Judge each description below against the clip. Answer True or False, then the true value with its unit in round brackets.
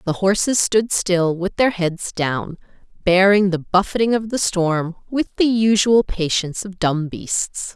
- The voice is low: False (195 Hz)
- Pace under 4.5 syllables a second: True (4.0 syllables/s)